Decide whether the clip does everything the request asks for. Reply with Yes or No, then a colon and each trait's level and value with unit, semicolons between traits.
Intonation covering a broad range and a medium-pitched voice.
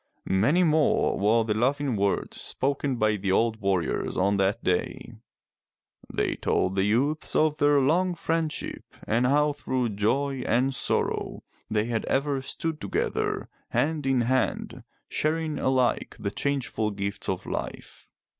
No: wide, 5.7 semitones; low, 130 Hz